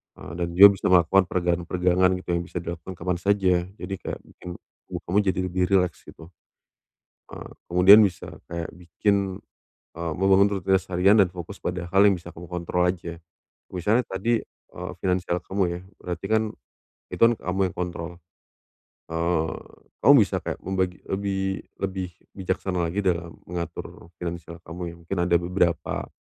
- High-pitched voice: No, very low, 90 Hz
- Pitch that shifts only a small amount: Yes, narrow, 1.9 semitones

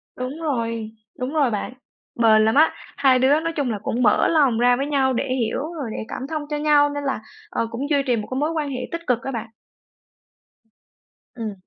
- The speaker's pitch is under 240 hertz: No, very high, 260 Hz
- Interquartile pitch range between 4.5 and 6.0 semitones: No, average, 4.0 semitones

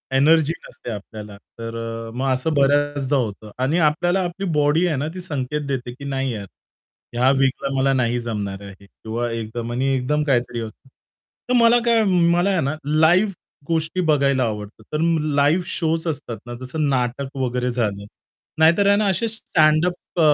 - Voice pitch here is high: No, medium, 140 Hz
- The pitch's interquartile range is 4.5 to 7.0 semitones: Yes, average, 5.2 semitones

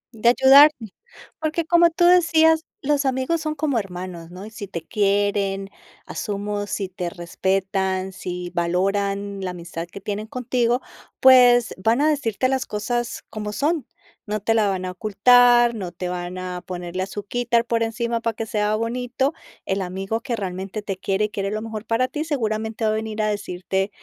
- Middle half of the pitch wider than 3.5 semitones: Yes, average, 4.2 semitones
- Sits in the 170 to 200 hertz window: No, high, 215 Hz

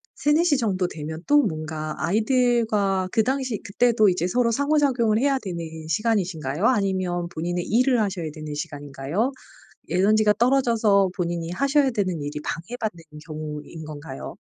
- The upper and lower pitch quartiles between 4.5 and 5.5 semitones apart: No, wide, 6.6 semitones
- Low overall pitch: No, high, 195 Hz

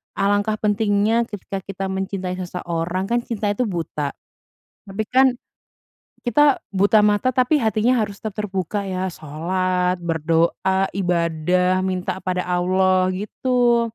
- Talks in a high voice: Yes, high, 195 Hz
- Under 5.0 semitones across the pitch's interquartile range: Yes, average, 2.9 semitones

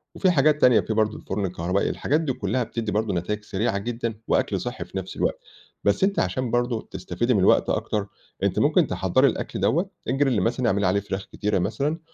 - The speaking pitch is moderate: No, low, 110 Hz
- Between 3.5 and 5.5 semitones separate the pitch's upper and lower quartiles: Yes, average, 4.3 semitones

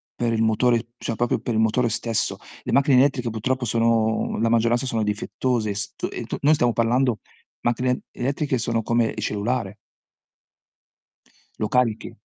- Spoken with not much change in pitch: Yes, narrow, 2.1 semitones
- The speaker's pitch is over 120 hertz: No, low, 115 Hz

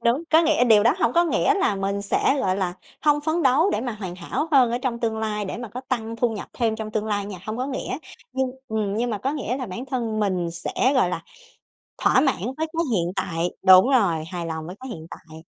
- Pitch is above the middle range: Yes, high, 220 Hz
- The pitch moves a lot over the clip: No, average, 5.0 semitones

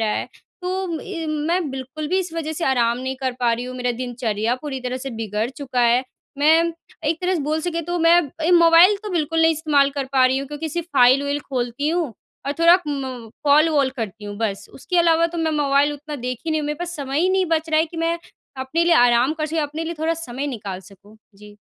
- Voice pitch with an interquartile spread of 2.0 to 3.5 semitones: No, average, 4.7 semitones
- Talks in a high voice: Yes, very high, 295 Hz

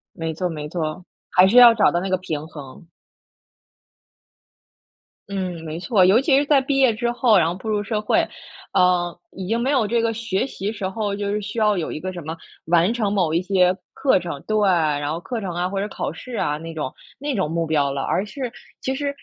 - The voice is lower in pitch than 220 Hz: Yes, high, 190 Hz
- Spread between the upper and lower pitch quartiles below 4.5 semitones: No, average, 5.2 semitones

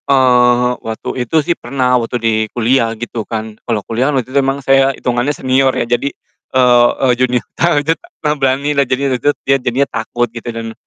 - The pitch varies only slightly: Yes, narrow, 2.2 semitones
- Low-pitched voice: Yes, low, 125 Hz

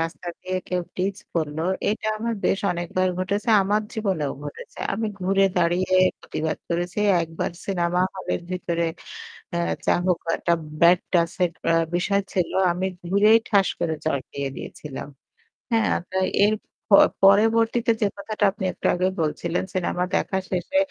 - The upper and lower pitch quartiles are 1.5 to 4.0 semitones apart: Yes, average, 2.8 semitones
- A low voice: No, medium, 185 Hz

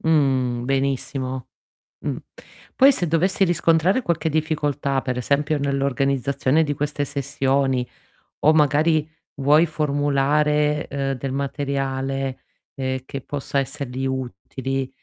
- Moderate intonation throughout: No, narrow, 2.0 semitones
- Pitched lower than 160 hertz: Yes, medium, 140 Hz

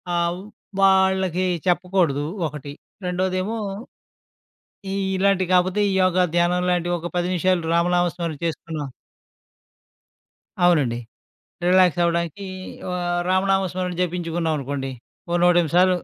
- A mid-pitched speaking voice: Yes, medium, 175 Hz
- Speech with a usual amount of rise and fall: No, narrow, 1.5 semitones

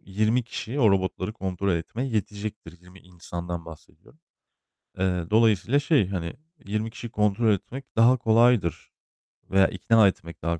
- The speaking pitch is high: No, low, 100 Hz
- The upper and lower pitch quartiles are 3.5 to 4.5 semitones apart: Yes, average, 4.1 semitones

